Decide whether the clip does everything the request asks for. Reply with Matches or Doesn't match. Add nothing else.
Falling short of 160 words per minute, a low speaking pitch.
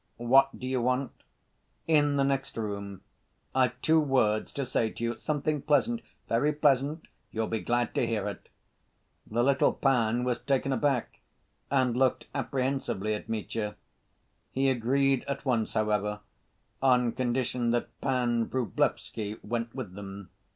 Matches